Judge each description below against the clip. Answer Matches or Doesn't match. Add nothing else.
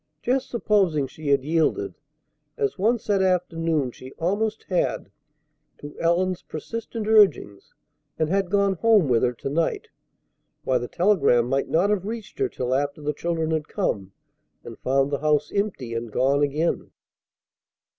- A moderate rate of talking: Matches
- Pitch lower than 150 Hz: Doesn't match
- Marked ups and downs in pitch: Matches